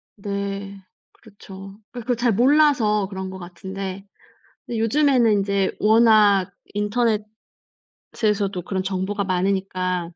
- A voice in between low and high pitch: No, high, 200 Hz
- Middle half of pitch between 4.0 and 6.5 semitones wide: No, narrow, 2.6 semitones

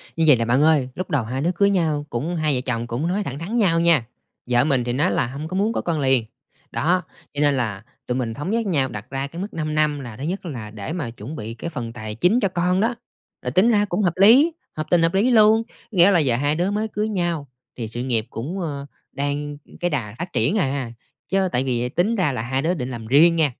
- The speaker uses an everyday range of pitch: No, wide, 6.3 semitones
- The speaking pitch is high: No, medium, 150 Hz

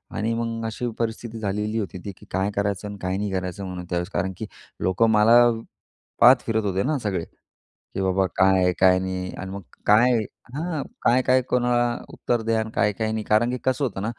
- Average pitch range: Yes, average, 3.7 semitones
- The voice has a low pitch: Yes, low, 105 Hz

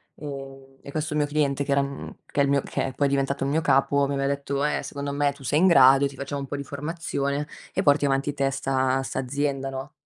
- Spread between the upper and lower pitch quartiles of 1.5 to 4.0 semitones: No, narrow, 0.9 semitones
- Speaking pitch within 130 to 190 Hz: Yes, medium, 140 Hz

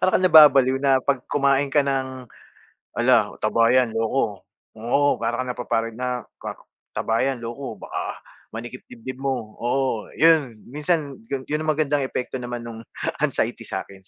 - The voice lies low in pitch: Yes, low, 130 Hz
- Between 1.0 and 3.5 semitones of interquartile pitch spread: Yes, average, 3.0 semitones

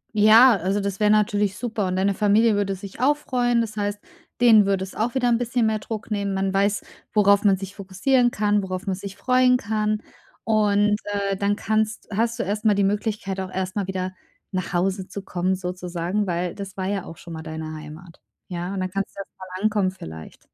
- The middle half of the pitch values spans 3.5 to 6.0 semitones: No, narrow, 2.4 semitones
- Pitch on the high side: Yes, high, 200 Hz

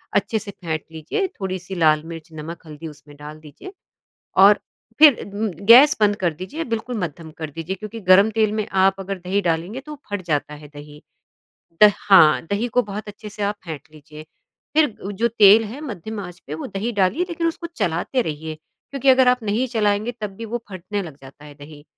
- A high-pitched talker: Yes, high, 195 Hz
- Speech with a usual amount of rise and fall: No, wide, 5.8 semitones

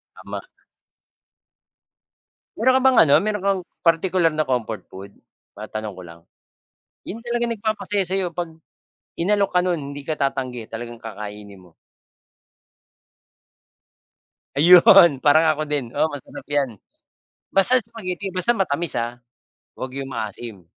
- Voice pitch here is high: No, medium, 155 Hz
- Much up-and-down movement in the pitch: Yes, wide, 8.6 semitones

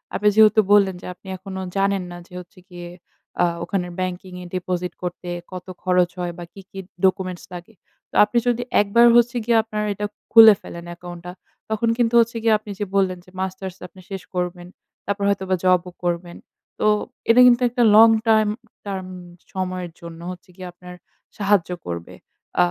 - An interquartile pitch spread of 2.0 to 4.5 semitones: Yes, average, 2.9 semitones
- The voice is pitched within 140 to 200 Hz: Yes, high, 190 Hz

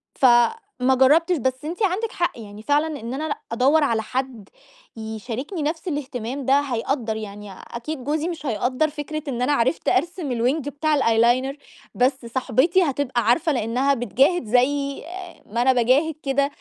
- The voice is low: No, very high, 265 Hz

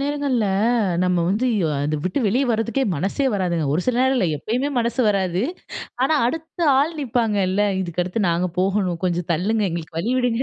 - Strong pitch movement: Yes, wide, 6.0 semitones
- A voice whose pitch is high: Yes, high, 210 Hz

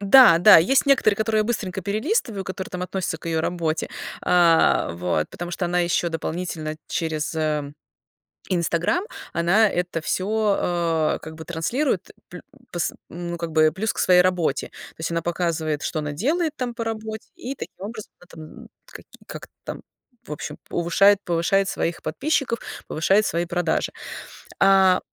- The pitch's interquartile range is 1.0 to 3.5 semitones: No, average, 4.3 semitones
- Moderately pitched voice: Yes, medium, 180 Hz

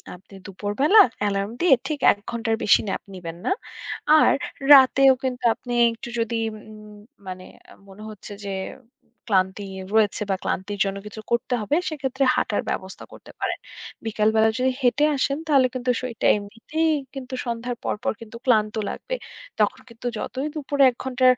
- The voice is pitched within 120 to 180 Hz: No, high, 230 Hz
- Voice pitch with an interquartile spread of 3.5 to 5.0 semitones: Yes, average, 4.1 semitones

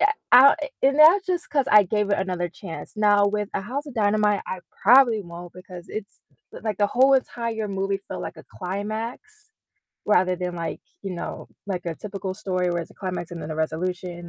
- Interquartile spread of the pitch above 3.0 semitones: Yes, average, 4.1 semitones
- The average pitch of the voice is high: Yes, high, 200 Hz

